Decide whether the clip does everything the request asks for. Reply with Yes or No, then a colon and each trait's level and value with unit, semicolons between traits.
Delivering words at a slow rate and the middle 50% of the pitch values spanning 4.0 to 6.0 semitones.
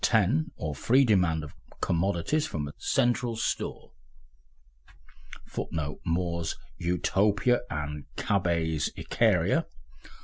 Yes: slow, 95 wpm; wide, 5.5 semitones